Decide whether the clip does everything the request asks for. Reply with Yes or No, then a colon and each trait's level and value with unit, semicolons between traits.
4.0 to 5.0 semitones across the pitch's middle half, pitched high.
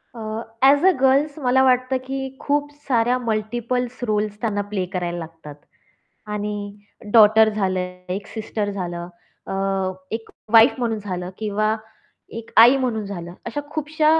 Yes: average, 4.3 semitones; high, 220 Hz